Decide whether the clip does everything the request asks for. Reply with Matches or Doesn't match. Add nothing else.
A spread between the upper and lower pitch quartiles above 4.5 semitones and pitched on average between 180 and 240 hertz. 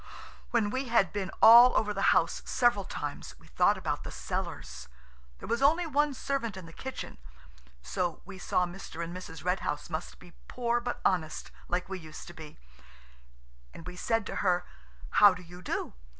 Matches